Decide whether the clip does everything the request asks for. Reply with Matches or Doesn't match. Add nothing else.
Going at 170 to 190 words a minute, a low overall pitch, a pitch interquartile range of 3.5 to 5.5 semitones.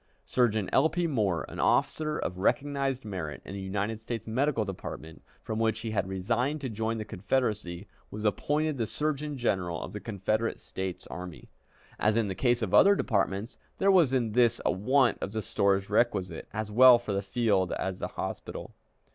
Matches